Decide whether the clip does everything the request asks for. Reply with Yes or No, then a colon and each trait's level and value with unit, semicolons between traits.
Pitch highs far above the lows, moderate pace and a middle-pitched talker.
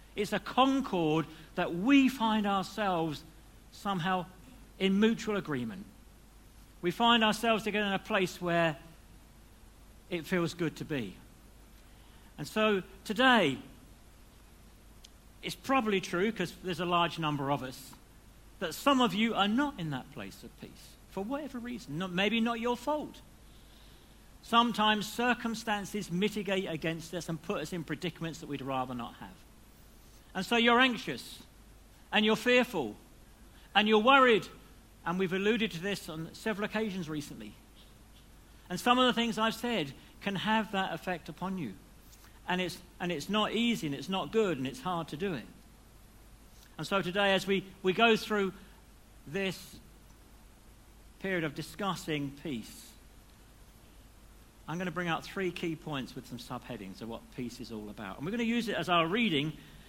Yes: wide, 7.1 semitones; average, 160 wpm; medium, 180 Hz